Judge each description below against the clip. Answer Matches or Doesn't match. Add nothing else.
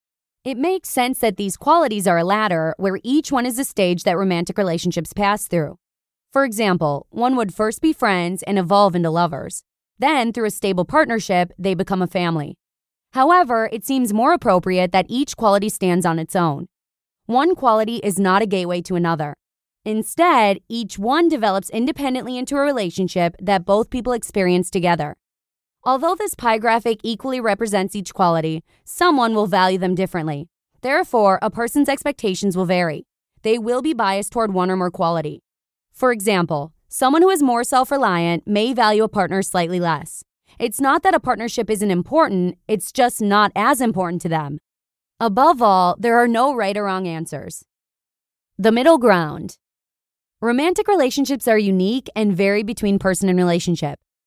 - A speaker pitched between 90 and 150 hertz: Doesn't match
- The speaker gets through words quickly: Doesn't match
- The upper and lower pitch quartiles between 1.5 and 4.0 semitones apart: Doesn't match